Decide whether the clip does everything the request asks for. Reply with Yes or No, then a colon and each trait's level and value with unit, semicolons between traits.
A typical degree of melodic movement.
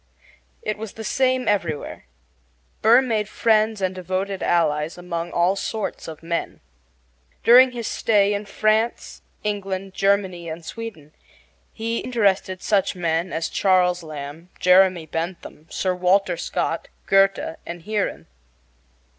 Yes: average, 3.8 semitones